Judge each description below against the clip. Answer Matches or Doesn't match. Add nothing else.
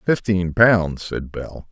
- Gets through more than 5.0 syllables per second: Doesn't match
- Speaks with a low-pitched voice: Matches